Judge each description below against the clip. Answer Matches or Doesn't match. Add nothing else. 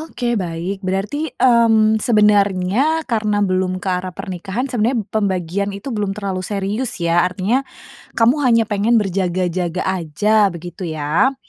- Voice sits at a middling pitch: Doesn't match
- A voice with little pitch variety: Doesn't match